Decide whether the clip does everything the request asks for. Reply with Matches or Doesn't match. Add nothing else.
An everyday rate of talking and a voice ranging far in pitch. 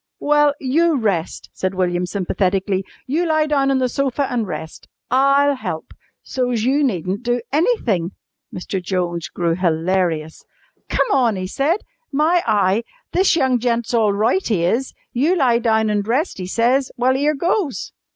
Matches